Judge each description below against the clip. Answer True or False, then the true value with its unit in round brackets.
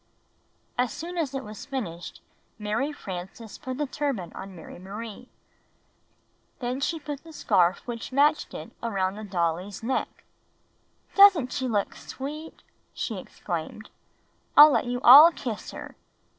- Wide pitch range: True (6.3 semitones)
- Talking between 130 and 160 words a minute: True (140 wpm)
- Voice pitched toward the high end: True (245 Hz)